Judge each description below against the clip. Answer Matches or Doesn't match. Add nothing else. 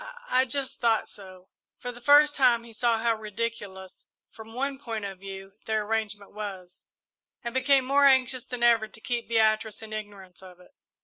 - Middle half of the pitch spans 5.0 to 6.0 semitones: Doesn't match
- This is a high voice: Matches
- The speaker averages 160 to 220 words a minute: Matches